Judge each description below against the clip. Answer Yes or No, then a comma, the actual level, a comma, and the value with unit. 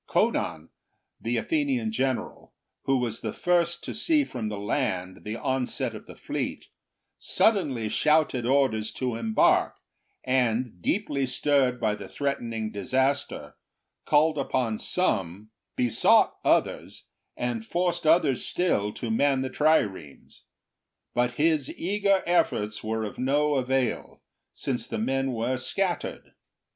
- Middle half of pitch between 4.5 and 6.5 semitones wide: Yes, average, 5.2 semitones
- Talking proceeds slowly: Yes, slow, 130 wpm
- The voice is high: No, low, 130 Hz